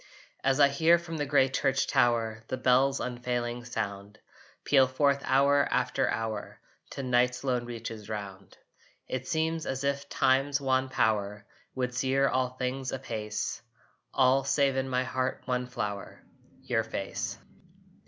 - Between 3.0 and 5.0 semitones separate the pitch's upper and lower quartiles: No, narrow, 2.4 semitones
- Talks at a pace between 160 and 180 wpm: No, average, 145 wpm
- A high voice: No, low, 130 Hz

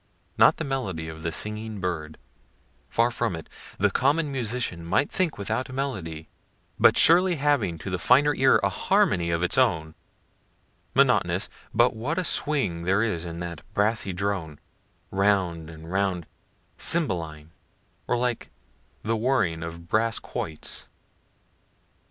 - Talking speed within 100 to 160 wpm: Yes, average, 140 wpm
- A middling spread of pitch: No, wide, 6.9 semitones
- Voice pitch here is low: Yes, low, 100 Hz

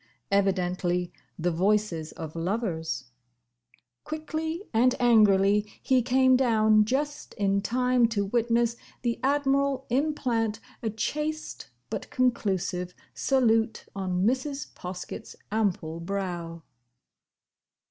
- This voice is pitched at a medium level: No, high, 220 Hz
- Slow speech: Yes, slow, 95 wpm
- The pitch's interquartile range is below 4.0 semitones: No, wide, 5.5 semitones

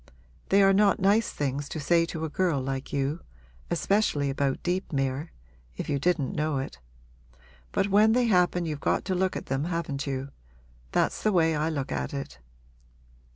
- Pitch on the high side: No, medium, 155 Hz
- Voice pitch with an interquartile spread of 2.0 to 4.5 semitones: No, average, 5.0 semitones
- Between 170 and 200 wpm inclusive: Yes, average, 175 wpm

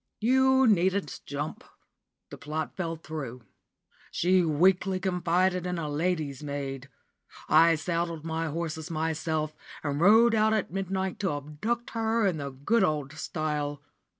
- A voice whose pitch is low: No, medium, 165 Hz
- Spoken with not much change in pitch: No, average, 3.9 semitones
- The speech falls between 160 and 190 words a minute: No, slow, 135 wpm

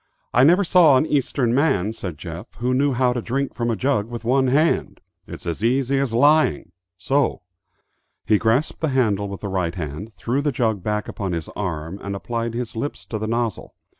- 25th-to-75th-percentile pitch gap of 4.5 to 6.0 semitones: Yes, average, 5.1 semitones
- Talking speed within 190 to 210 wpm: Yes, average, 200 wpm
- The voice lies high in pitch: No, low, 115 Hz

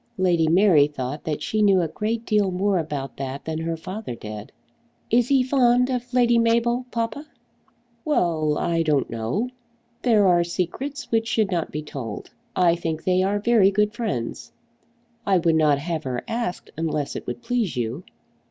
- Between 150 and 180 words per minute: Yes, average, 170 wpm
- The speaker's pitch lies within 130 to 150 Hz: No, medium, 185 Hz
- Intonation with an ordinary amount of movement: No, wide, 6.8 semitones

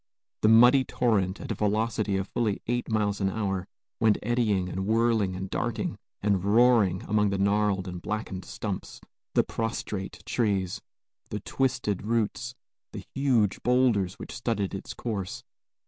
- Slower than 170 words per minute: Yes, average, 145 wpm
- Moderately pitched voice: No, low, 105 Hz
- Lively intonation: No, average, 3.2 semitones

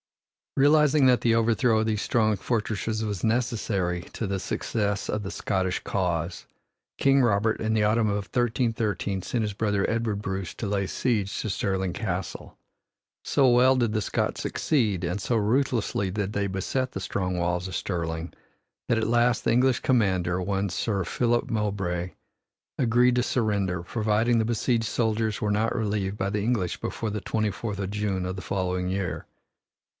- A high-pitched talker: No, low, 105 Hz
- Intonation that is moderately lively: Yes, average, 3.3 semitones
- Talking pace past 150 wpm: Yes, average, 170 wpm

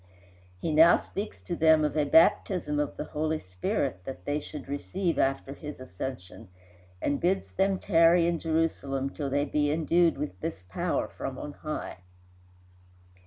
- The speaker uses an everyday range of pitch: Yes, average, 3.3 semitones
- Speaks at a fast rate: No, average, 160 wpm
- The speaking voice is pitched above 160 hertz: No, medium, 150 Hz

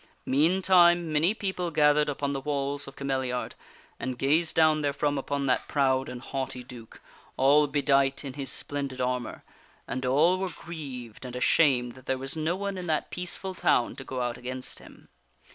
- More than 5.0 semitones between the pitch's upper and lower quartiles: No, average, 3.3 semitones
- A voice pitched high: No, medium, 140 Hz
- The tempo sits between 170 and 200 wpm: Yes, average, 175 wpm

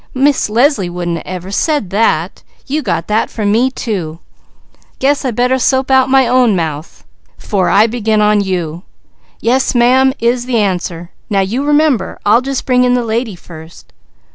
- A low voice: No, high, 225 Hz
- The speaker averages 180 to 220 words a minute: No, average, 165 wpm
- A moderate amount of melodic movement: No, wide, 5.7 semitones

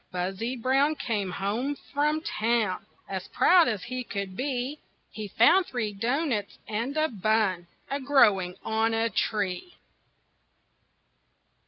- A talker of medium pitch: No, high, 230 Hz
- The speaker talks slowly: Yes, slow, 125 wpm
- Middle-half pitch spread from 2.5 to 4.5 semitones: No, wide, 5.4 semitones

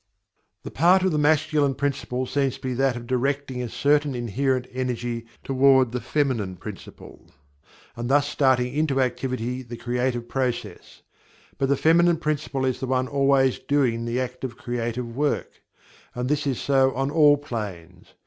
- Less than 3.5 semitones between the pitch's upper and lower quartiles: Yes, narrow, 2.6 semitones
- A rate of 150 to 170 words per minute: Yes, average, 160 wpm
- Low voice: Yes, low, 130 Hz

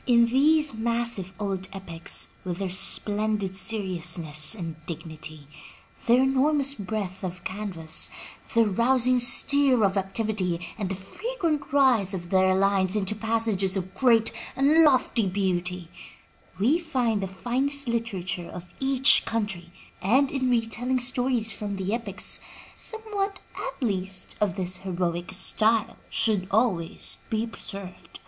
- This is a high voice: Yes, high, 210 Hz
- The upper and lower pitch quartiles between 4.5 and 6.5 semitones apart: Yes, average, 5.0 semitones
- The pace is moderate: No, slow, 130 wpm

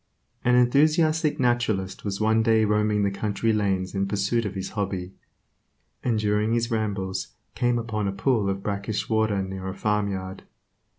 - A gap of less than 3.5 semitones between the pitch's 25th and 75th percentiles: Yes, average, 2.7 semitones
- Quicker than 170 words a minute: No, average, 160 wpm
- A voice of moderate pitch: No, low, 105 Hz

